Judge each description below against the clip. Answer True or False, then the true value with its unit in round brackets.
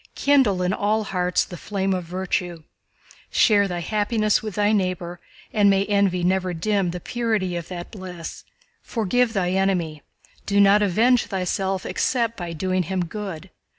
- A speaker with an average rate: True (155 wpm)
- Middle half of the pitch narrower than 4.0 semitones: True (2.7 semitones)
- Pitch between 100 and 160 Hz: False (190 Hz)